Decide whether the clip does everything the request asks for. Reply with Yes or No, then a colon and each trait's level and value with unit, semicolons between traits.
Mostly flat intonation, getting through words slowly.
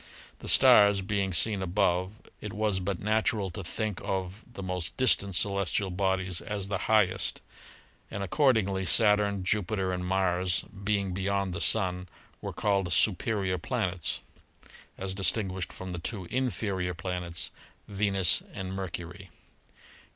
Yes: narrow, 2.0 semitones; slow, 130 wpm